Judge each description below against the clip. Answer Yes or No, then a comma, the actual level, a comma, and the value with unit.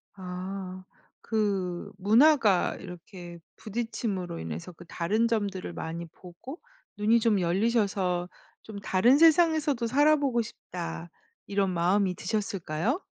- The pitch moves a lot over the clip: No, average, 4.5 semitones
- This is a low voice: No, high, 200 Hz